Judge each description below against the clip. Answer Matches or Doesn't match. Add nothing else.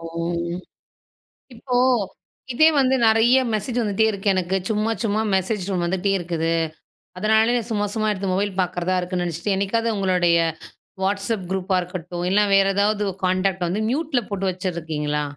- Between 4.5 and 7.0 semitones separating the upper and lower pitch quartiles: Doesn't match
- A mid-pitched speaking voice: Doesn't match